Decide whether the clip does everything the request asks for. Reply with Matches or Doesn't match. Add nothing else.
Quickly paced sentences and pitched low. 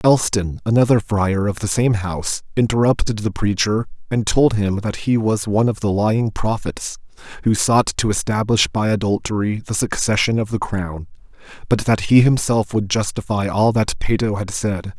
Doesn't match